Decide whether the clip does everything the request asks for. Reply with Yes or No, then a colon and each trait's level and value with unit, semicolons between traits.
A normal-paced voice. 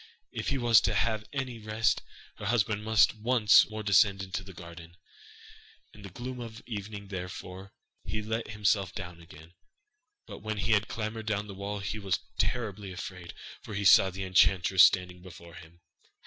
Yes: average, 175 wpm